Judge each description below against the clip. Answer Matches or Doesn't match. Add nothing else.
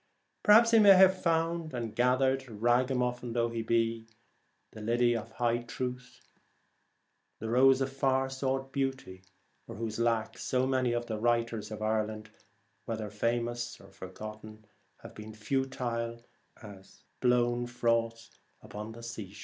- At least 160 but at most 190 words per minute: Doesn't match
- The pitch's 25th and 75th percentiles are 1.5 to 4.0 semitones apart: Matches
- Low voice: Matches